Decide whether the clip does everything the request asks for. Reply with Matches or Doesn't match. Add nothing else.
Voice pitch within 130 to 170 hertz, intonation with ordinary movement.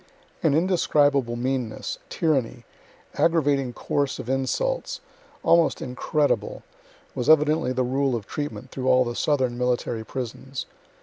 Matches